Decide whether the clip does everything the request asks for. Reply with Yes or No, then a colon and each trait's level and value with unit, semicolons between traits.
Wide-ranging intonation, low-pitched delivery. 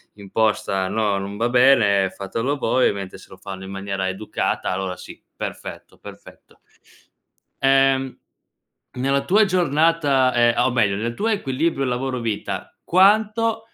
Yes: wide, 5.8 semitones; low, 125 Hz